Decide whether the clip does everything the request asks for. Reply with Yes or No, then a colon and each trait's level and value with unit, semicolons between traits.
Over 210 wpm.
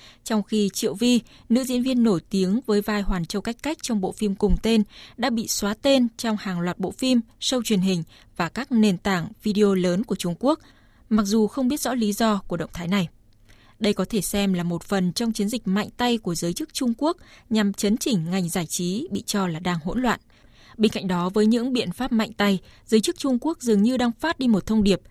Yes: average, 245 wpm